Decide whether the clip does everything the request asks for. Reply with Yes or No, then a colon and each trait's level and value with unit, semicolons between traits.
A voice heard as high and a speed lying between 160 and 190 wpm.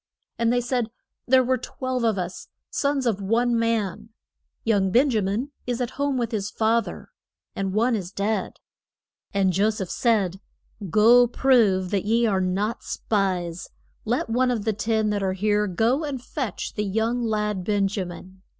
Yes: high, 220 Hz; average, 175 wpm